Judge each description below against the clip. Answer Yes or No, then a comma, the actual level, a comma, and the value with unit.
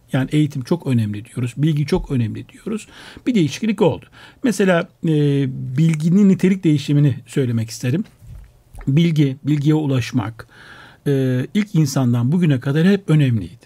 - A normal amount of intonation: Yes, average, 4.7 semitones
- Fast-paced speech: No, average, 125 wpm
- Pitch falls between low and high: Yes, medium, 145 Hz